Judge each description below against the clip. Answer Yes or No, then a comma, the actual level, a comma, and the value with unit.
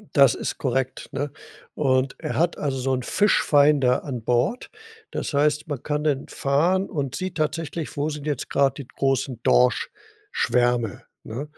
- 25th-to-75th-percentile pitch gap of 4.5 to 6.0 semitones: No, average, 2.8 semitones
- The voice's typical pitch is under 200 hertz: Yes, medium, 140 Hz